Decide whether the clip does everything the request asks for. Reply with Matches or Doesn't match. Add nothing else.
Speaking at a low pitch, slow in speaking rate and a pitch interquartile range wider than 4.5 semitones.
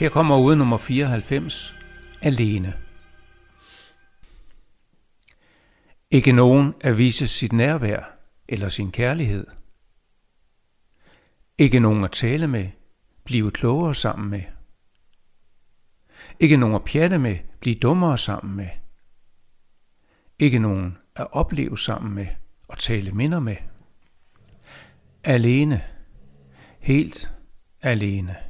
Matches